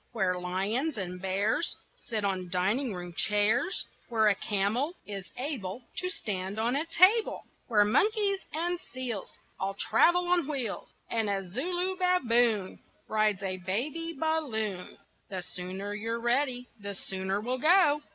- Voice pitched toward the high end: Yes, high, 220 Hz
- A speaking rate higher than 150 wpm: No, average, 140 wpm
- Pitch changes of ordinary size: No, wide, 7.6 semitones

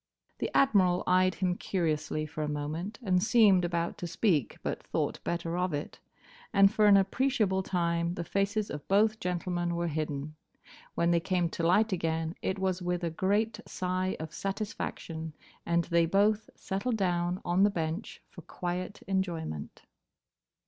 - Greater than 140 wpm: Yes, average, 160 wpm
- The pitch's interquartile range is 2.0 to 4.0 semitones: Yes, average, 2.8 semitones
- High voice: No, medium, 180 Hz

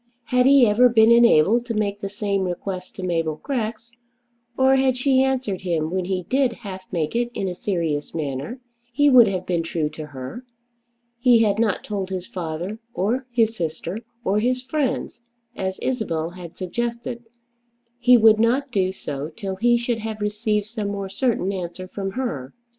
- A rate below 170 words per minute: No, average, 175 wpm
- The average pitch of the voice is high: Yes, high, 210 Hz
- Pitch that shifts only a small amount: No, average, 4.8 semitones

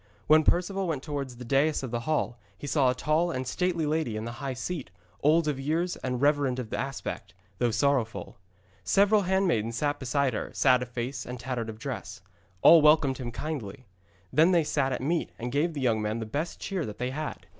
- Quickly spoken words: Yes, fast, 210 wpm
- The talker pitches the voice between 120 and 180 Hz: Yes, medium, 140 Hz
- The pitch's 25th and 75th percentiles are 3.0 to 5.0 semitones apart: Yes, average, 4.2 semitones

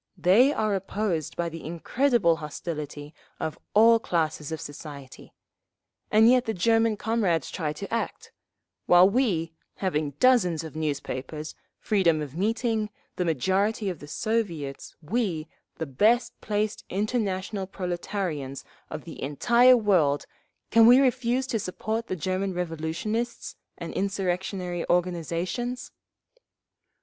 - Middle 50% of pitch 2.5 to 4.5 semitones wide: No, wide, 5.6 semitones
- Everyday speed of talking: No, slow, 120 wpm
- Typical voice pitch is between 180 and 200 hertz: Yes, medium, 185 Hz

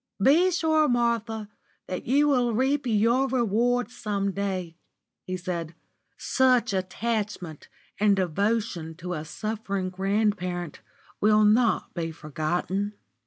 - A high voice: Yes, high, 205 Hz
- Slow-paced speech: Yes, slow, 115 wpm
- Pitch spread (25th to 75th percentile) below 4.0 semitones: No, average, 4.5 semitones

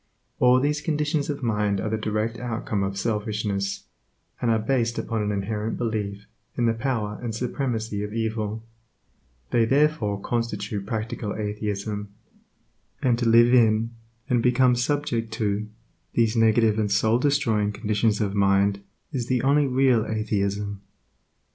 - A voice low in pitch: Yes, low, 110 Hz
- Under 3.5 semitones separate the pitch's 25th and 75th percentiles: Yes, average, 2.7 semitones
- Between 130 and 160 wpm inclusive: Yes, average, 140 wpm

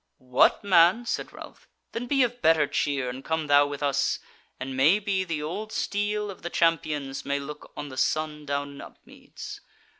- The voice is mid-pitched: Yes, medium, 155 Hz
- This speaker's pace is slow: No, average, 185 wpm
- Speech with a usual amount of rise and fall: No, wide, 5.7 semitones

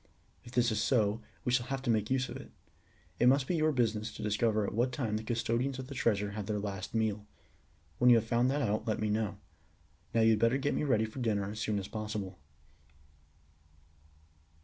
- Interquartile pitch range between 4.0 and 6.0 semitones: No, average, 2.9 semitones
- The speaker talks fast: Yes, fast, 215 wpm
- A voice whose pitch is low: Yes, low, 110 Hz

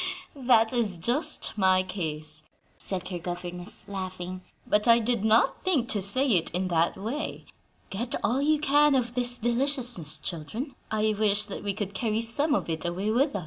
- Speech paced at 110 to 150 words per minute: No, average, 180 wpm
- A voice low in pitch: No, high, 215 Hz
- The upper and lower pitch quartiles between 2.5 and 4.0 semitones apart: No, average, 5.0 semitones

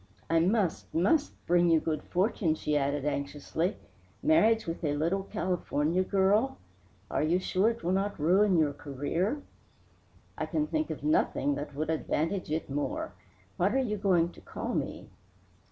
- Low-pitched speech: No, medium, 175 Hz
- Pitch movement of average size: Yes, average, 5.0 semitones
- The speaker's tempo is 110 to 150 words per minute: No, average, 160 wpm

